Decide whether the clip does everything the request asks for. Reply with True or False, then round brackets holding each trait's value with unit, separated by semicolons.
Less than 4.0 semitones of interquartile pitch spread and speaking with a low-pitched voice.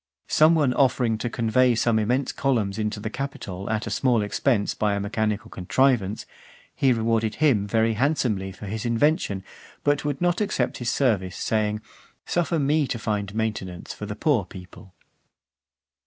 False (4.4 semitones; 110 Hz)